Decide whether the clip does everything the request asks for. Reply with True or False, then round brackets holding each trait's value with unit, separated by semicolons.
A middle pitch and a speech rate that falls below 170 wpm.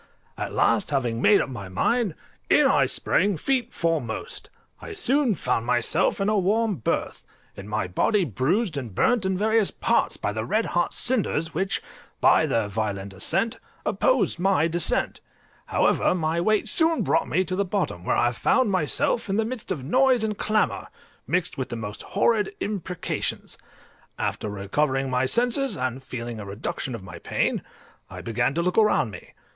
False (175 Hz; 175 wpm)